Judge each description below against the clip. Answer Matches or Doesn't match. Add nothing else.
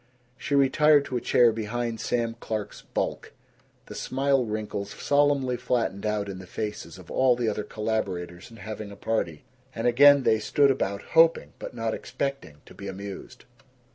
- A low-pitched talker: Matches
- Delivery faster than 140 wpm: Matches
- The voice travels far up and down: Doesn't match